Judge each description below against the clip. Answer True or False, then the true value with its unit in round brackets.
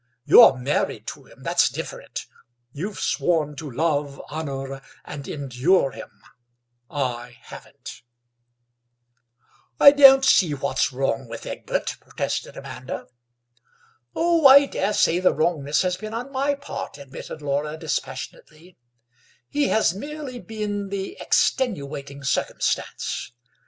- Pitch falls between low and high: True (160 Hz)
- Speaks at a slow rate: True (110 wpm)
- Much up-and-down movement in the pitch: True (8.0 semitones)